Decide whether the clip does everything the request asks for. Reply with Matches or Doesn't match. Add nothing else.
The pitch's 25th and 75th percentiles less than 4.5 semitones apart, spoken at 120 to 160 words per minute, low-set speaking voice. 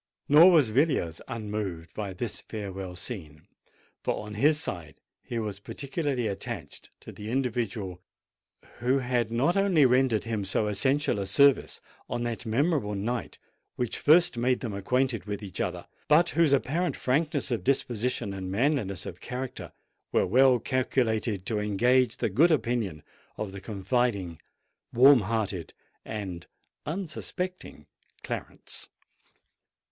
Doesn't match